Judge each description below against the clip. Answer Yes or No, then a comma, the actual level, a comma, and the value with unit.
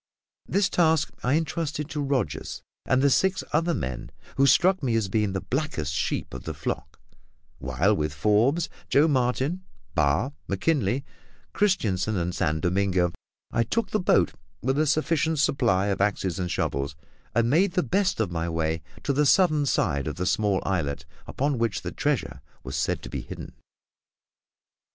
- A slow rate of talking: No, average, 165 wpm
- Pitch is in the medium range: No, low, 120 Hz